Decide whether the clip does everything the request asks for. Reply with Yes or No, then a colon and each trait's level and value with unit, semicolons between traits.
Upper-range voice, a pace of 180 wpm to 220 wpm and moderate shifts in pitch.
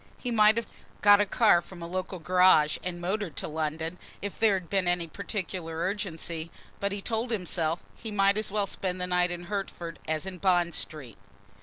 No: medium, 180 Hz; average, 195 wpm; average, 3.0 semitones